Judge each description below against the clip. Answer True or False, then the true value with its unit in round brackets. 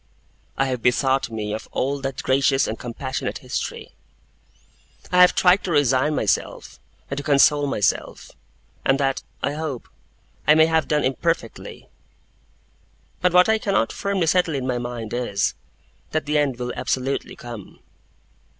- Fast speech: False (150 wpm)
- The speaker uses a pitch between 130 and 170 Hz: True (135 Hz)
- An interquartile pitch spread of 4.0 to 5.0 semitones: True (4.3 semitones)